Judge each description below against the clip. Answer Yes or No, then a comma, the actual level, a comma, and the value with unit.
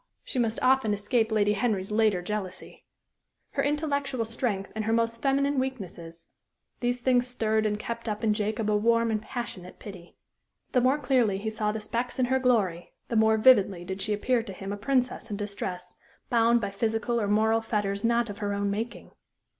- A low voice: No, high, 220 Hz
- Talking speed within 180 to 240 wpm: Yes, average, 190 wpm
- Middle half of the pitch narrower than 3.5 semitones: Yes, average, 3.0 semitones